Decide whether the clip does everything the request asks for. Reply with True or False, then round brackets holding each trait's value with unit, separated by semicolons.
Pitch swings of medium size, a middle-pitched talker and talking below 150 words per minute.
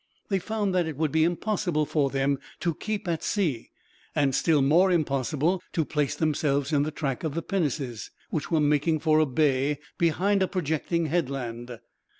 False (3.6 semitones; 155 Hz; 175 wpm)